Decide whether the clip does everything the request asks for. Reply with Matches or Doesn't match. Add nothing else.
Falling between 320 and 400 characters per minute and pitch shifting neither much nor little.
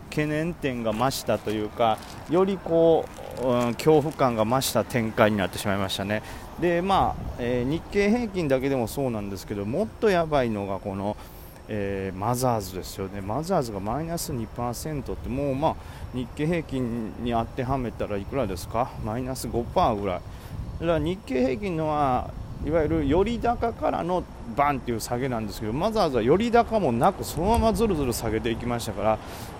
Doesn't match